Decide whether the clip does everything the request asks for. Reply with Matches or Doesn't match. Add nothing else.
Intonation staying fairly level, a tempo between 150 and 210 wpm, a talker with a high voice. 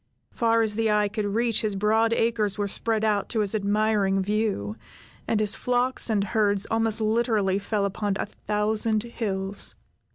Matches